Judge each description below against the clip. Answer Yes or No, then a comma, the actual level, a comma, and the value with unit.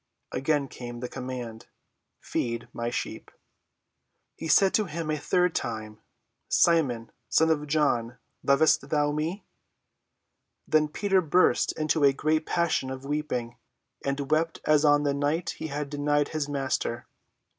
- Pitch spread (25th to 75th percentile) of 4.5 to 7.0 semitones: No, average, 3.2 semitones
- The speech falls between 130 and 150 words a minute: Yes, average, 140 wpm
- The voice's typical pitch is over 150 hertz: No, medium, 145 Hz